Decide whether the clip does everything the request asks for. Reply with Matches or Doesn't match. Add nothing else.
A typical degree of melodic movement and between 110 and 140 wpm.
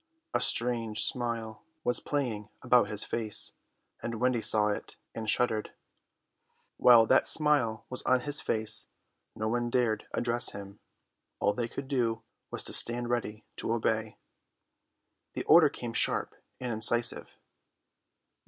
Doesn't match